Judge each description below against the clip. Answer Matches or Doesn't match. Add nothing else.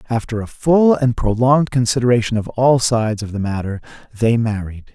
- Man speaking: Matches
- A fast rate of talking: Doesn't match